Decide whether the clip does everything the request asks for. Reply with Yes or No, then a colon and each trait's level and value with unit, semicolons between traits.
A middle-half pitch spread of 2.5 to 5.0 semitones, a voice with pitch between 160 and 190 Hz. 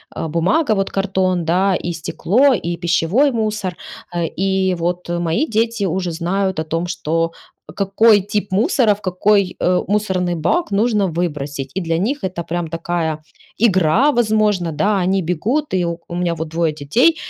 Yes: average, 3.7 semitones; medium, 185 Hz